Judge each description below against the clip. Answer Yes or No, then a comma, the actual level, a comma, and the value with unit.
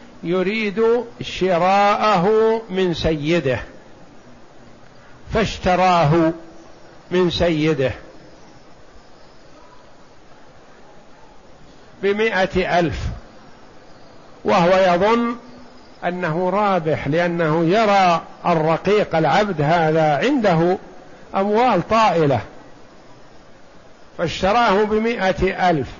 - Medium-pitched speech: Yes, medium, 180 Hz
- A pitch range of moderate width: Yes, average, 3.8 semitones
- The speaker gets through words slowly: Yes, slow, 55 wpm